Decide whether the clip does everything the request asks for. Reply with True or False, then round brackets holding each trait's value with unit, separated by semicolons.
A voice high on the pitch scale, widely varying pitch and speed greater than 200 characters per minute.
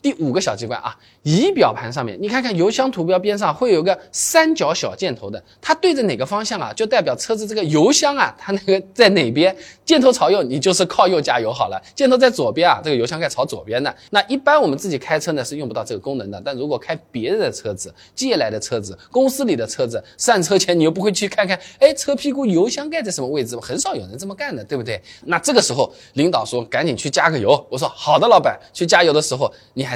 True (230 Hz; 6.8 semitones; 370 characters per minute)